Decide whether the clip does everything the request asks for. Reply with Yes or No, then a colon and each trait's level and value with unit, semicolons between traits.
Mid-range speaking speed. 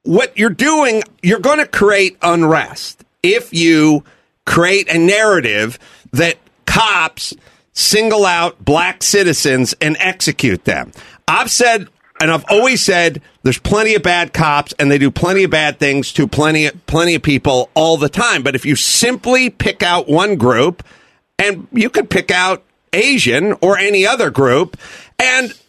Yes: average, 155 wpm